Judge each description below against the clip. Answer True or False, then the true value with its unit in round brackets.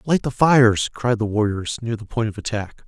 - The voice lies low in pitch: True (115 Hz)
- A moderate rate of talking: False (230 wpm)